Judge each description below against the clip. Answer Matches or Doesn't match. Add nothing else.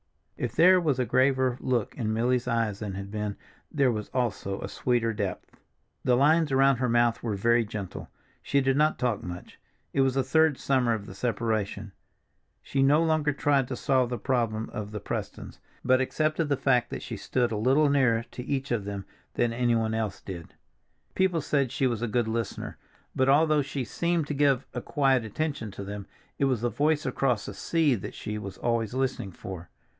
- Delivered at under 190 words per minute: Doesn't match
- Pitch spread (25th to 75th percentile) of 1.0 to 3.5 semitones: Doesn't match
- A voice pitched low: Matches